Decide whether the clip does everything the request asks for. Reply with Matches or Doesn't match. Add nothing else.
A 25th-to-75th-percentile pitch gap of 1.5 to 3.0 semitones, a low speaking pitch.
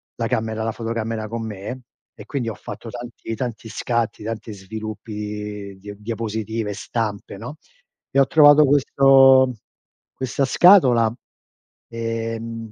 Matches